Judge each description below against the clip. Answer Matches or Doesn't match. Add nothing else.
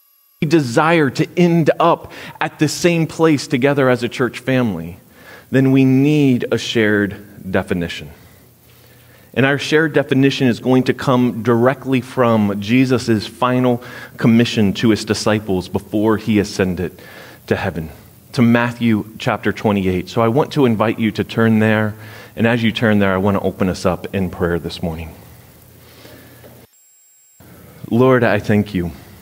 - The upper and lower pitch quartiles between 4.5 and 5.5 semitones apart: Doesn't match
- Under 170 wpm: Matches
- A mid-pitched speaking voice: Doesn't match